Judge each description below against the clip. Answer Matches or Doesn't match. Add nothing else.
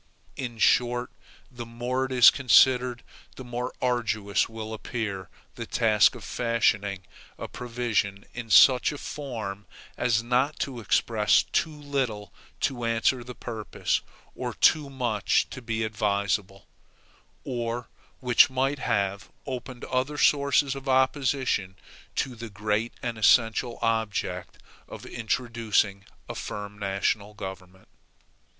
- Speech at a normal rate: Doesn't match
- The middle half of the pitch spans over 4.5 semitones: Doesn't match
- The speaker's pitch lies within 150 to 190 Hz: Doesn't match